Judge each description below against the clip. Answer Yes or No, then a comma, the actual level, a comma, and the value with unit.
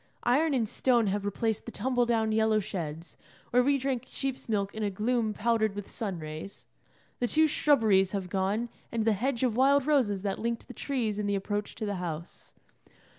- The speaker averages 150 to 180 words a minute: No, average, 195 wpm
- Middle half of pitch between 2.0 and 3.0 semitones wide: No, average, 3.6 semitones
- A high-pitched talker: Yes, high, 220 Hz